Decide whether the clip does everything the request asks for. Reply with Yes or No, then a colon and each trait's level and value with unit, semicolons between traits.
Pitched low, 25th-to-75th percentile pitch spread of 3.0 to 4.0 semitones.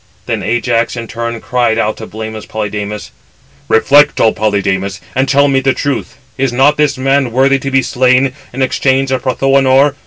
Yes: low, 130 Hz; average, 3.4 semitones